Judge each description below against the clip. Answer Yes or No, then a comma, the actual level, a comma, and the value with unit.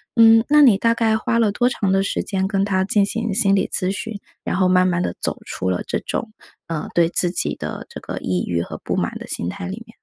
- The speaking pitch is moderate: No, high, 195 Hz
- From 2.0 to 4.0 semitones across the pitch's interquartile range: Yes, average, 3.6 semitones